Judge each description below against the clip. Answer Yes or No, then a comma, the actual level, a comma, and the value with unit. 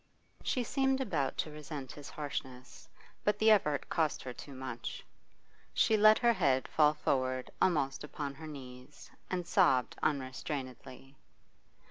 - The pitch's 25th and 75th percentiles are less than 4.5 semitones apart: No, average, 4.9 semitones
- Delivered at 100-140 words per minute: Yes, slow, 135 wpm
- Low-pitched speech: No, medium, 145 Hz